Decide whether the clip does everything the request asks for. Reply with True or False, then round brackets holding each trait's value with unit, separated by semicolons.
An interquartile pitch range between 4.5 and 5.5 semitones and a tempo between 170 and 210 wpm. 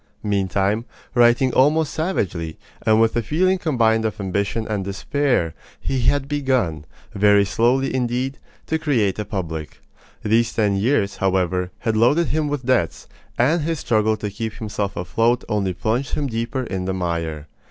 False (5.1 semitones; 155 wpm)